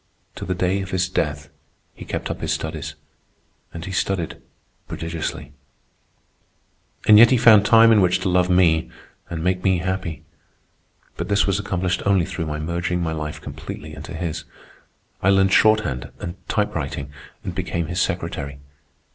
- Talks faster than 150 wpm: Yes, average, 160 wpm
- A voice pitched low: Yes, very low, 90 Hz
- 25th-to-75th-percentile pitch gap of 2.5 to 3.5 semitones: Yes, average, 3.0 semitones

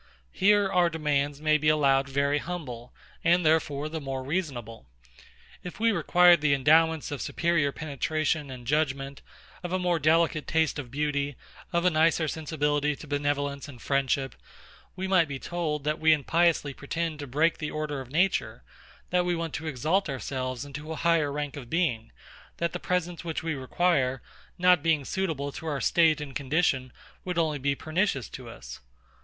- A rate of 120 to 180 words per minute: Yes, average, 170 wpm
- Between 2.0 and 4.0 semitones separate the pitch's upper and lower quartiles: Yes, average, 3.1 semitones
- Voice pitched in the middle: Yes, medium, 150 Hz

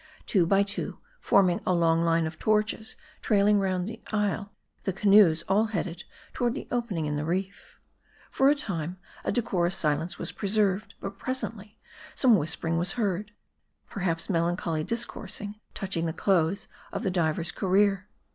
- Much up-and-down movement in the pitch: No, average, 3.8 semitones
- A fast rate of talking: No, average, 165 wpm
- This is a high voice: Yes, high, 195 Hz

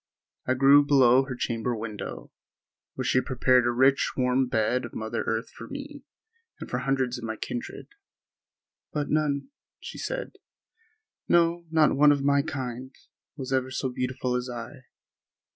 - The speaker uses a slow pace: No, average, 160 wpm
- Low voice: Yes, low, 130 Hz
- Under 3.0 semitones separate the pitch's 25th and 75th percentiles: Yes, narrow, 2.5 semitones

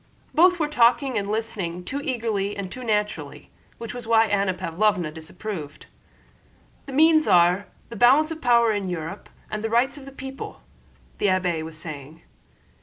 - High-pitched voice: Yes, high, 215 Hz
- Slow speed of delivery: No, average, 165 wpm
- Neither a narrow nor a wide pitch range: No, wide, 5.8 semitones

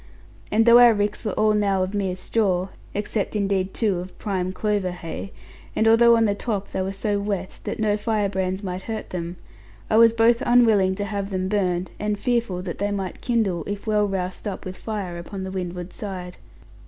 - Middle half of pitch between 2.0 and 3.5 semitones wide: Yes, narrow, 2.5 semitones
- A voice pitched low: No, high, 200 Hz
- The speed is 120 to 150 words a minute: No, average, 200 wpm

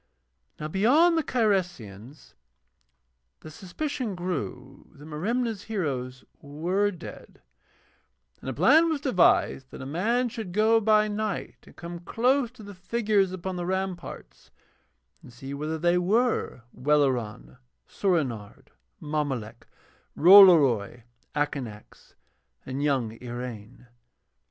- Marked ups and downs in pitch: Yes, wide, 8.0 semitones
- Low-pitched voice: No, medium, 175 Hz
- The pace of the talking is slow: Yes, slow, 115 wpm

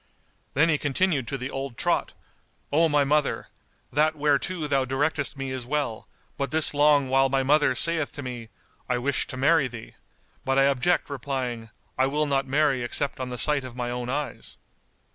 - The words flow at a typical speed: Yes, average, 185 wpm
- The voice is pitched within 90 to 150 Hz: Yes, medium, 140 Hz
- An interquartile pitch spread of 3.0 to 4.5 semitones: No, narrow, 2.5 semitones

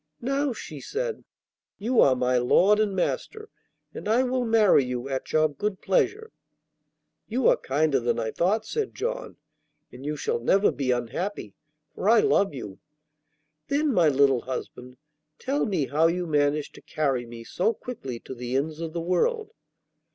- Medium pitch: Yes, medium, 165 Hz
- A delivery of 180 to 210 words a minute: No, average, 165 wpm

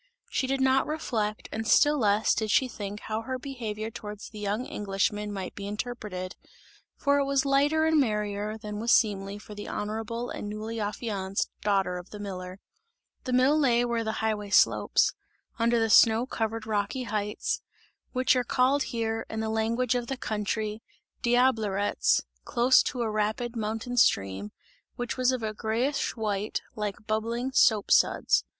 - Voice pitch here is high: Yes, high, 220 Hz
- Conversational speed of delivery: Yes, average, 165 wpm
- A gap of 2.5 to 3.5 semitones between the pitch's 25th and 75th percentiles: Yes, average, 2.9 semitones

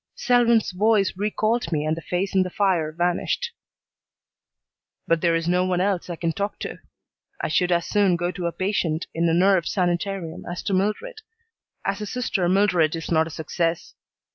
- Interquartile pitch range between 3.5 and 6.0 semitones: No, average, 3.1 semitones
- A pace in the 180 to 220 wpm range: Yes, average, 185 wpm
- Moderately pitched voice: Yes, medium, 180 Hz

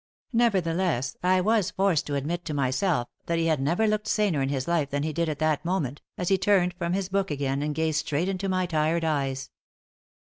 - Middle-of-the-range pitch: Yes, medium, 165 Hz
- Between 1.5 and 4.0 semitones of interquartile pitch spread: No, average, 4.5 semitones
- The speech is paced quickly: Yes, fast, 215 wpm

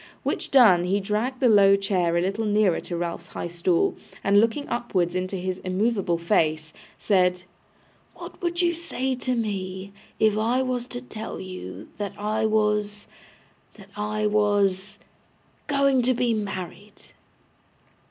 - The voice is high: Yes, high, 205 Hz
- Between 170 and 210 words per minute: No, average, 145 wpm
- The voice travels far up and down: No, average, 3.7 semitones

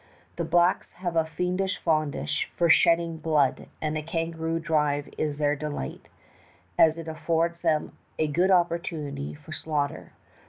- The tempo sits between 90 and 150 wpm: Yes, average, 145 wpm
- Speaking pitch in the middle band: Yes, medium, 160 Hz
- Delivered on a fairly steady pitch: Yes, narrow, 1.9 semitones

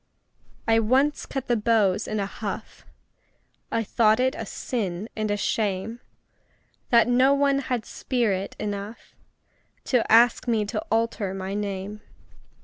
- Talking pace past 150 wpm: No, average, 140 wpm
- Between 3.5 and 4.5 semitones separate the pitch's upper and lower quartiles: No, average, 3.1 semitones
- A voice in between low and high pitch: No, high, 220 Hz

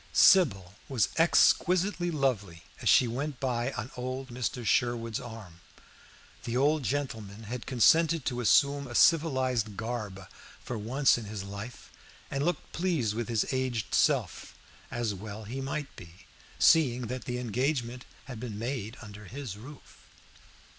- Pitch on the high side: No, low, 125 Hz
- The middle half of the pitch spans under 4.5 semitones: Yes, average, 3.9 semitones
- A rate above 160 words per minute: No, average, 145 wpm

